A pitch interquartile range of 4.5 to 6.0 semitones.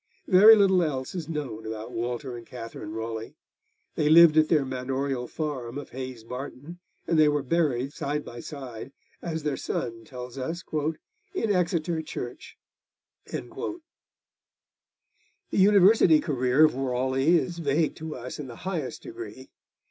Yes: average, 4.8 semitones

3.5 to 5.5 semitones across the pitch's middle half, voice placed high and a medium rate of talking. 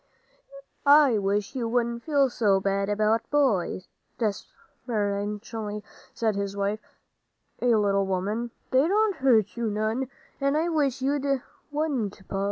No: average, 5.0 semitones; high, 225 Hz; slow, 125 wpm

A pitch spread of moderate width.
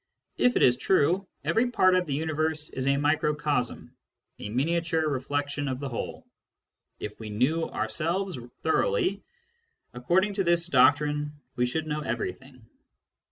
Yes: average, 4.5 semitones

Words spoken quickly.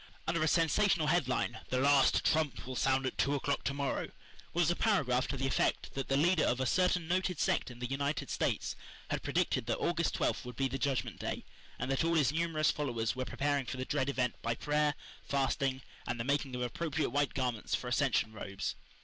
Yes: fast, 210 wpm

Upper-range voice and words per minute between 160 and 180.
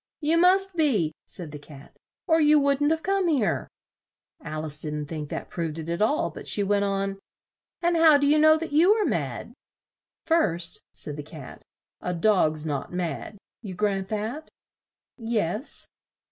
Yes: high, 205 Hz; average, 170 wpm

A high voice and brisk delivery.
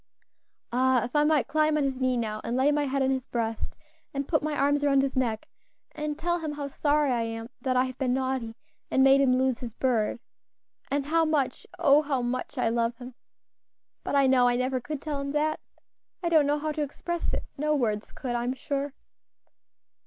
Yes: very high, 270 Hz; fast, 215 wpm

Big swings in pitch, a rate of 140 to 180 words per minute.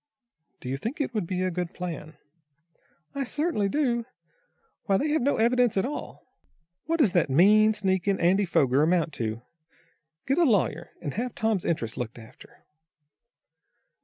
Yes: wide, 6.6 semitones; average, 160 wpm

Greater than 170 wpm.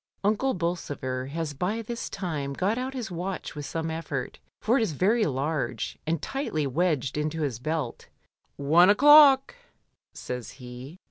No: average, 150 wpm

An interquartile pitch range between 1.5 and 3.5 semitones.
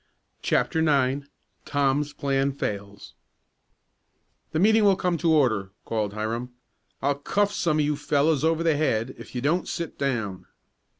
No: average, 4.7 semitones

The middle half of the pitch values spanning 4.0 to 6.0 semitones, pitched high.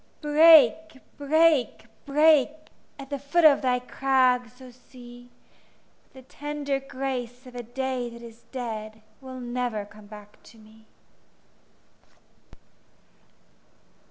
No: average, 2.7 semitones; very high, 255 Hz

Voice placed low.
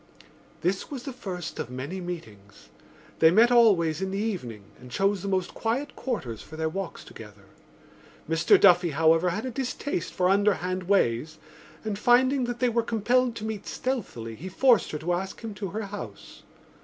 No: high, 190 Hz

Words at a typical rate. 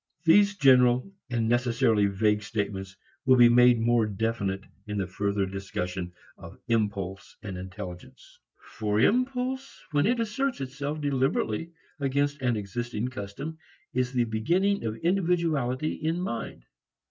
No: slow, 130 wpm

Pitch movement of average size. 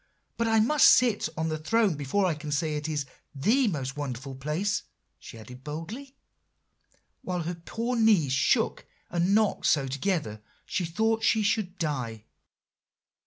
No: wide, 7.0 semitones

